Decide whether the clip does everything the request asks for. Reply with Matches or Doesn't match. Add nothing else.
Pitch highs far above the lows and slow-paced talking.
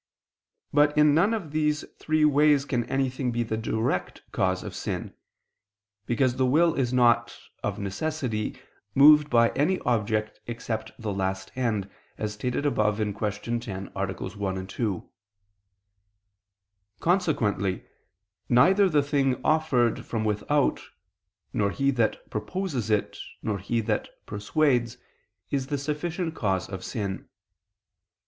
Matches